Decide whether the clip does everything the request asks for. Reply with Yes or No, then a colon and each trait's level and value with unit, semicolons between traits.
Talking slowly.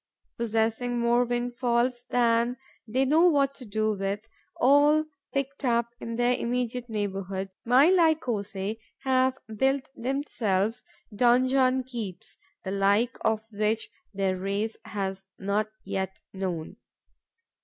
Yes: slow, 115 wpm